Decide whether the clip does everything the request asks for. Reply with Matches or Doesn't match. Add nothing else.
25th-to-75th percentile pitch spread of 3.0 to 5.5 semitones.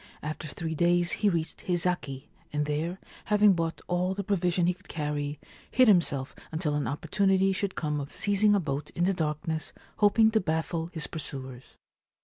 Matches